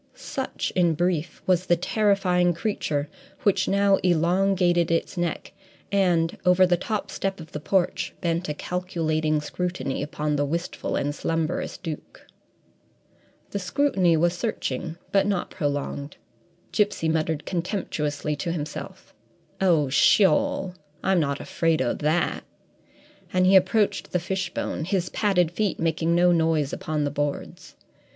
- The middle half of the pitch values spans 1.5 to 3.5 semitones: Yes, average, 3.2 semitones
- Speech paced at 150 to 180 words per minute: No, slow, 135 wpm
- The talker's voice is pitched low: No, medium, 175 Hz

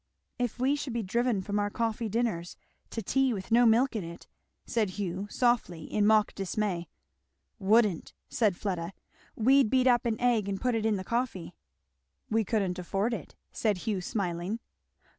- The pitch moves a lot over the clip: No, average, 3.8 semitones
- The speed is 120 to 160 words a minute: No, average, 170 wpm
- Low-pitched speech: No, high, 215 Hz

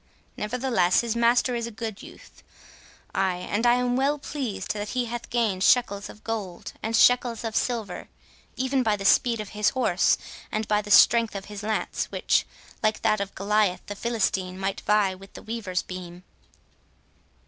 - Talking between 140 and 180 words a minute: Yes, average, 170 wpm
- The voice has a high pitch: Yes, high, 215 Hz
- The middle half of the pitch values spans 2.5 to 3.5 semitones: Yes, average, 3.2 semitones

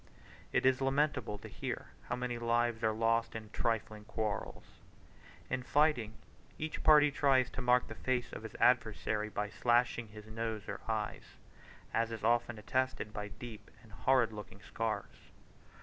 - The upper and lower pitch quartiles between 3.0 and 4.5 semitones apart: No, narrow, 2.5 semitones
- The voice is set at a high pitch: No, low, 115 Hz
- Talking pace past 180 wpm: No, average, 155 wpm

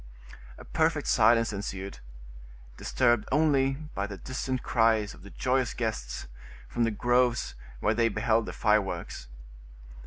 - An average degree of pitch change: Yes, average, 3.3 semitones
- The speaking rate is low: Yes, slow, 130 wpm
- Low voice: Yes, low, 115 Hz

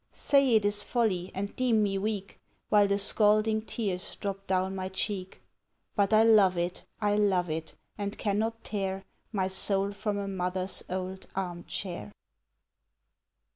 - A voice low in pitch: No, high, 200 Hz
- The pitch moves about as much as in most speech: No, narrow, 1.9 semitones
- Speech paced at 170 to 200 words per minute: No, average, 150 wpm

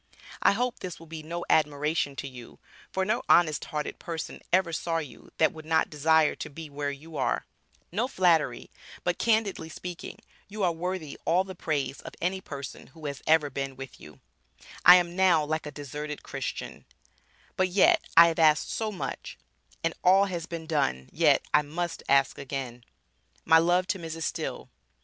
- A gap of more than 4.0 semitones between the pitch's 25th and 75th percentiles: No, average, 3.3 semitones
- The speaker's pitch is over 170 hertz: No, medium, 160 Hz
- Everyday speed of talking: Yes, average, 180 wpm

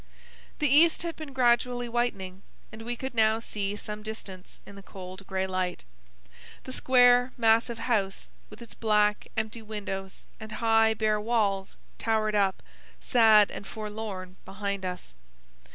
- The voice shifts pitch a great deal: No, average, 3.1 semitones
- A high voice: Yes, high, 215 Hz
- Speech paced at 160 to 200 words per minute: No, average, 145 wpm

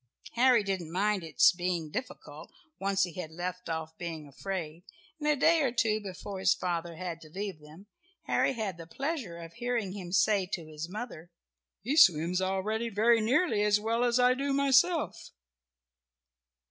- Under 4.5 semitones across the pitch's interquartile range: No, wide, 5.6 semitones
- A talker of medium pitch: No, high, 195 Hz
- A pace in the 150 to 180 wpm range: Yes, average, 170 wpm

